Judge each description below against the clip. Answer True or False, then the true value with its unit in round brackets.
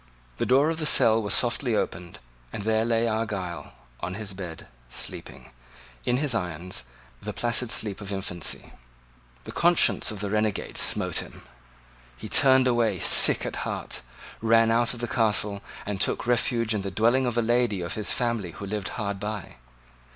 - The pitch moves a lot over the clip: False (3.3 semitones)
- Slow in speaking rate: False (175 wpm)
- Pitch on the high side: False (110 Hz)